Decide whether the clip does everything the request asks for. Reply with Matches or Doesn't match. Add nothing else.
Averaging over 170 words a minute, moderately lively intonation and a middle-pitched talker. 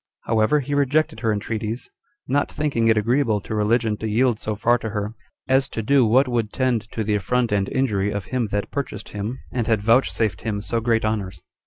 Doesn't match